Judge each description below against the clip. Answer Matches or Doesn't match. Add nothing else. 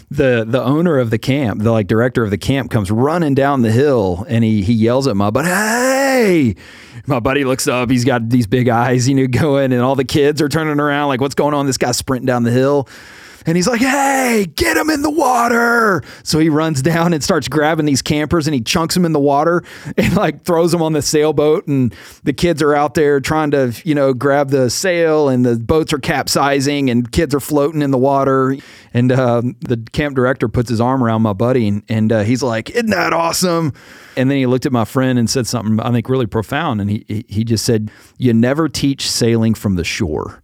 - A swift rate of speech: Matches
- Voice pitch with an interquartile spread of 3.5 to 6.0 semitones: Matches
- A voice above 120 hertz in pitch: Matches